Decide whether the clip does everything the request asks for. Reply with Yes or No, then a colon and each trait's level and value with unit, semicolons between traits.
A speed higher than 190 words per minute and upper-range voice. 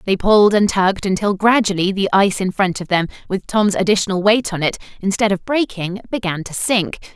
Yes: average, 200 wpm; high, 195 Hz